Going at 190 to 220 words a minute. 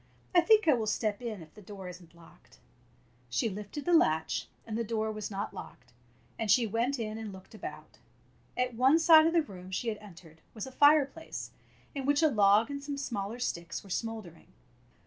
Yes: fast, 205 wpm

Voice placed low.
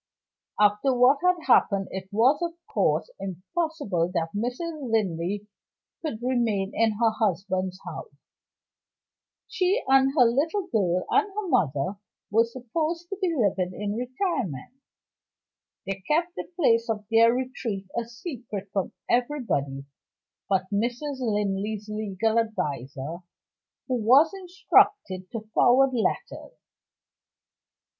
No: high, 230 Hz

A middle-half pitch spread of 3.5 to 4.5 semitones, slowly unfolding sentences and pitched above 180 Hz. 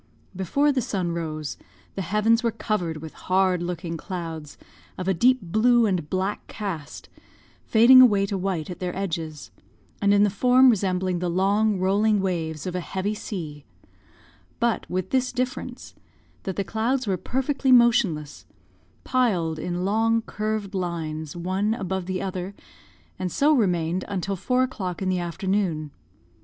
No: average, 4.0 semitones; average, 150 wpm; high, 190 Hz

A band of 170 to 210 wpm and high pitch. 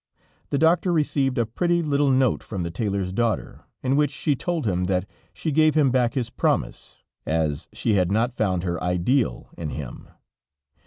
No: average, 175 wpm; low, 120 Hz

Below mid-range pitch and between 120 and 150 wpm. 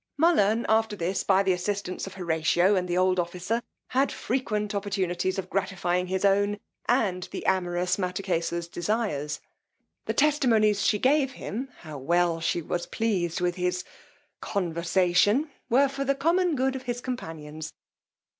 No: high, 190 Hz; average, 145 wpm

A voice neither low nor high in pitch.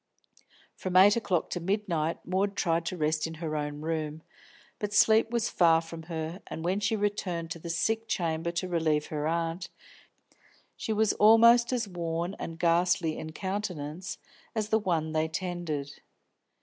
Yes: medium, 170 Hz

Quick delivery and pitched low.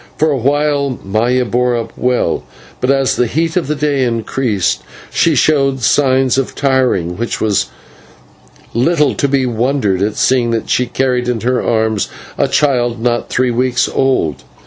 No: average, 165 wpm; low, 125 Hz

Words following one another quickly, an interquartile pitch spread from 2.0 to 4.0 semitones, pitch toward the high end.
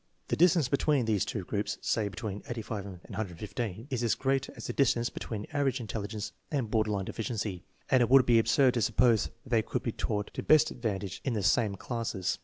No: fast, 210 wpm; average, 3.5 semitones; low, 115 Hz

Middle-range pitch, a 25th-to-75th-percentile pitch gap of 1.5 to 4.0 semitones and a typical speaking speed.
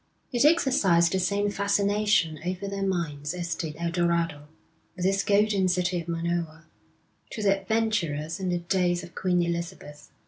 Yes: medium, 180 Hz; average, 2.8 semitones; average, 160 wpm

